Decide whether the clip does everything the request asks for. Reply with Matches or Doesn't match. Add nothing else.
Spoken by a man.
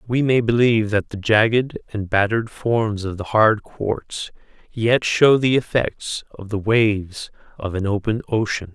Matches